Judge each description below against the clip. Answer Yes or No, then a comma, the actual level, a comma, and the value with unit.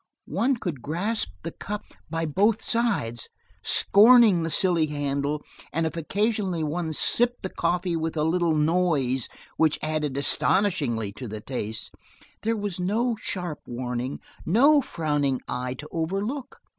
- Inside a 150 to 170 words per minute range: No, average, 140 wpm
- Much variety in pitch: Yes, wide, 6.1 semitones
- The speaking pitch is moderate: Yes, medium, 165 Hz